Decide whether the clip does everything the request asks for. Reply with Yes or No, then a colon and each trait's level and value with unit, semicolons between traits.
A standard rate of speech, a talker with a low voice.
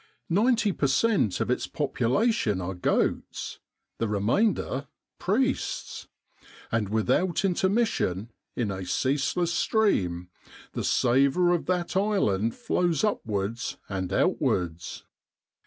No: slow, 105 wpm; low, 130 Hz